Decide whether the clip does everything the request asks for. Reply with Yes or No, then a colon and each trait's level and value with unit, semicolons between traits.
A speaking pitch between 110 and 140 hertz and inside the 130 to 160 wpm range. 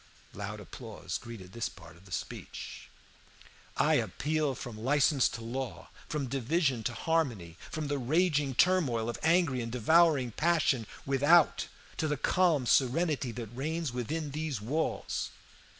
Yes: low, 135 Hz; average, 140 wpm